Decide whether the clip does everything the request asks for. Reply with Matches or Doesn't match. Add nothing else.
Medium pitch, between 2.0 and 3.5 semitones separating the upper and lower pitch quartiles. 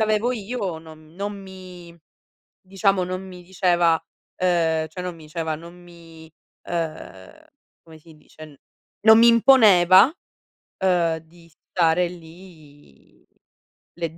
Matches